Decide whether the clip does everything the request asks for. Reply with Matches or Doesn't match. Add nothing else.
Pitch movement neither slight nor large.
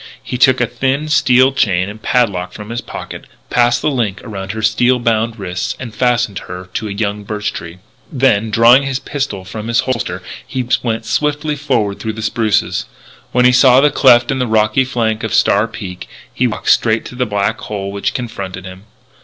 Matches